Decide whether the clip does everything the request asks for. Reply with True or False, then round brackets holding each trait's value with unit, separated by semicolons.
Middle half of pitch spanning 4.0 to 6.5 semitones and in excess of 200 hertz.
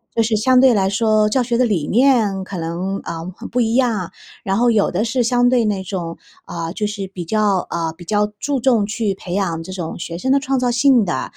True (4.6 semitones; 210 Hz)